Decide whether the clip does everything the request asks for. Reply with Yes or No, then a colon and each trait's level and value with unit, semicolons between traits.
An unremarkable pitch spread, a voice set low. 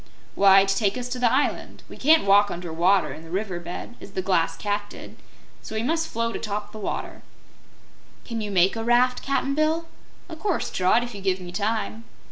No: average, 4.1 semitones; high, 210 Hz